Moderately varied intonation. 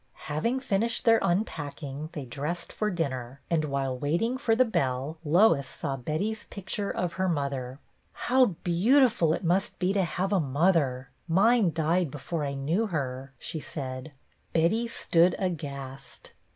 No: wide, 5.9 semitones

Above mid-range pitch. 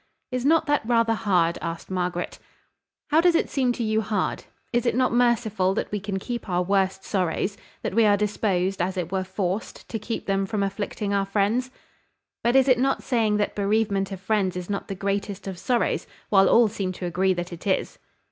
Yes: high, 200 Hz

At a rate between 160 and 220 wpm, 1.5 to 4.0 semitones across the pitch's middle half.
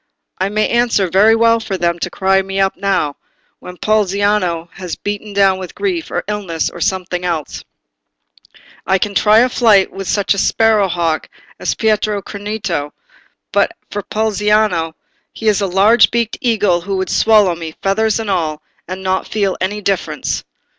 Yes: average, 165 wpm; average, 2.7 semitones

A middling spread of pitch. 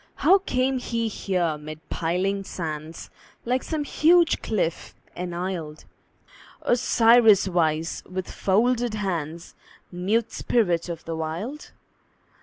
No: wide, 6.1 semitones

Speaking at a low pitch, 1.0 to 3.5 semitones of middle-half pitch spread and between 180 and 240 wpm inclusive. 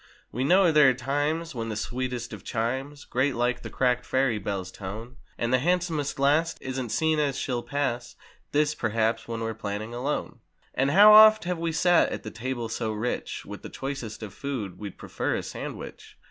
No: low, 130 Hz; average, 4.5 semitones; average, 195 wpm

